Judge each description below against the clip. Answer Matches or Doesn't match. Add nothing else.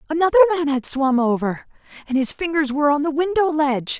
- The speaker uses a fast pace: Doesn't match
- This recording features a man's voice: Doesn't match